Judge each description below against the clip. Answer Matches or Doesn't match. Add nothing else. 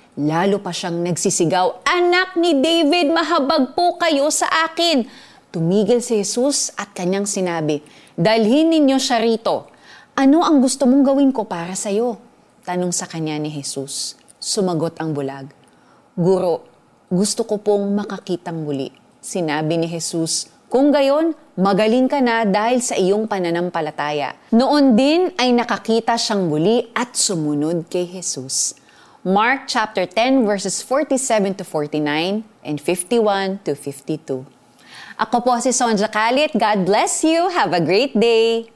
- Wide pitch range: Matches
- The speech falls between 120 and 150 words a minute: Matches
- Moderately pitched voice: Doesn't match